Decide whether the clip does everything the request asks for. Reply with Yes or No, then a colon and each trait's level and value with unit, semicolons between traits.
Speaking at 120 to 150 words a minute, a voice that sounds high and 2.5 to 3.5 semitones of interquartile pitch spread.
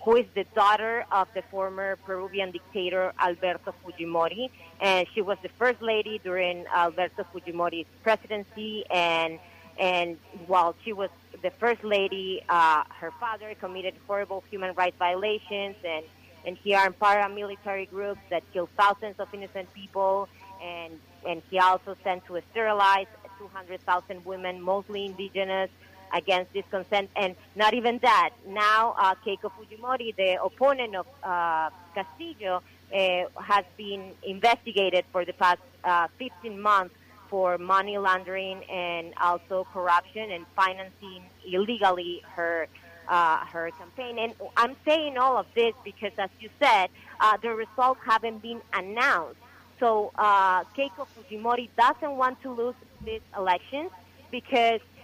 Yes: average, 140 wpm; high, 195 Hz; average, 3.0 semitones